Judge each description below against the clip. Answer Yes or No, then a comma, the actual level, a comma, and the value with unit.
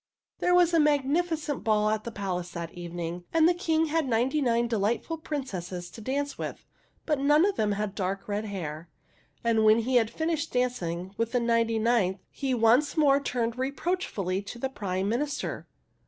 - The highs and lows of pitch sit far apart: Yes, wide, 6.4 semitones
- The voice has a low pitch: No, high, 235 Hz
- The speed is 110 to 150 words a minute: No, average, 180 wpm